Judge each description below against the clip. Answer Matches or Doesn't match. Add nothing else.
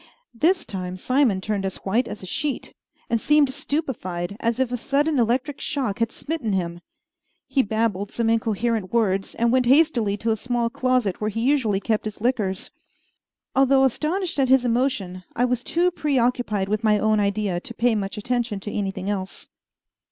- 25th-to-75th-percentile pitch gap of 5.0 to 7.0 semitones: Doesn't match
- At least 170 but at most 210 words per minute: Matches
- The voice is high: Matches